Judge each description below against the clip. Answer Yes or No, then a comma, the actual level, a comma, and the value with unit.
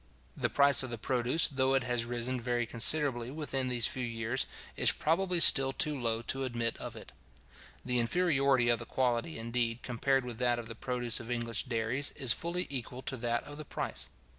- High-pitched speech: No, low, 125 Hz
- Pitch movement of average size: No, narrow, 2.3 semitones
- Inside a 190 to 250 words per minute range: Yes, average, 195 wpm